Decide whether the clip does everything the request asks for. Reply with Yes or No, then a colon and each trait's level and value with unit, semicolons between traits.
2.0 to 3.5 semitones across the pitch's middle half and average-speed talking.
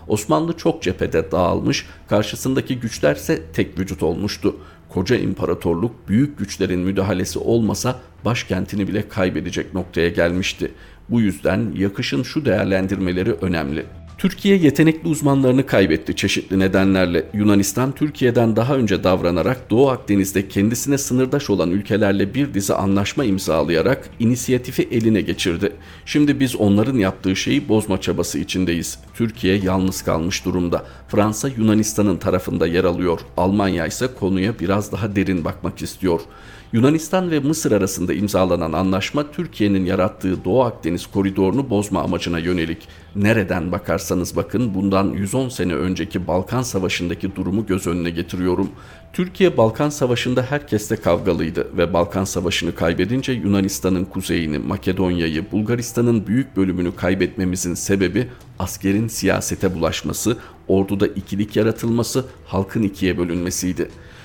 No: average, 4.3 semitones; average, 120 wpm